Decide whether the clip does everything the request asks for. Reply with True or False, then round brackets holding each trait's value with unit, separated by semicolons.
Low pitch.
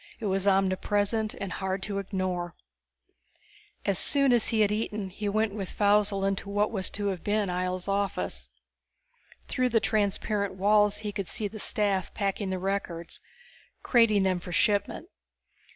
False (200 Hz)